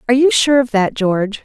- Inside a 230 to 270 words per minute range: Yes, fast, 250 wpm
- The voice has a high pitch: Yes, high, 235 Hz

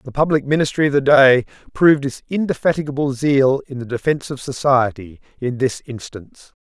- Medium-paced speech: Yes, average, 165 wpm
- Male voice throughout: Yes, male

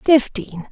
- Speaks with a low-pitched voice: No, very high, 260 Hz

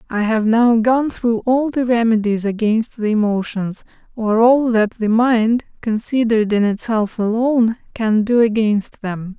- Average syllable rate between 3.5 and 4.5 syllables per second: Yes, 4.2 syllables/s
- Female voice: Yes, female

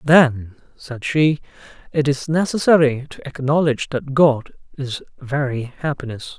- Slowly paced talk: Yes, slow, 120 wpm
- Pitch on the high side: No, medium, 140 Hz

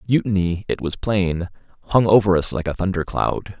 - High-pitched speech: No, very low, 95 Hz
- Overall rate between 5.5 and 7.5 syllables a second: No, 5.1 syllables/s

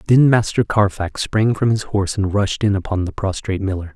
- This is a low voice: Yes, low, 100 Hz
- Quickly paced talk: Yes, fast, 210 wpm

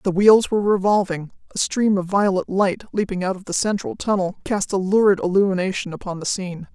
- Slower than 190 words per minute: No, average, 195 wpm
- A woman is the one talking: Yes, female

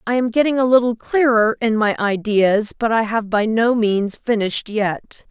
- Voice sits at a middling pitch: No, high, 225 Hz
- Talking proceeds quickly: No, average, 190 wpm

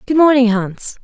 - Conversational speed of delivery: Yes, average, 175 wpm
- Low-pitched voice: No, high, 245 Hz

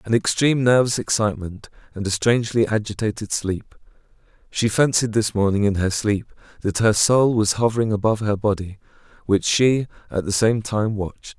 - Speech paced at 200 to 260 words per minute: No, average, 165 wpm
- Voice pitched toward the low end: Yes, low, 105 Hz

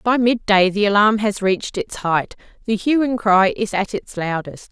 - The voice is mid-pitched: No, high, 215 Hz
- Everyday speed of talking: Yes, average, 190 wpm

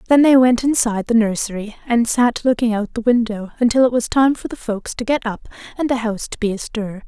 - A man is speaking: No, female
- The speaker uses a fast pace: Yes, fast, 235 wpm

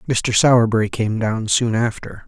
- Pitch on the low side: Yes, low, 110 Hz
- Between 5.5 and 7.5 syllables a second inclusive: No, 4.8 syllables/s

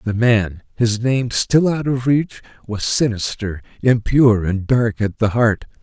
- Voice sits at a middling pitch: No, low, 115 Hz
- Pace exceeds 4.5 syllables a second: No, 4.0 syllables/s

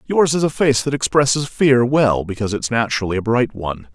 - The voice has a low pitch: Yes, low, 125 Hz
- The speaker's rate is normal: No, fast, 215 wpm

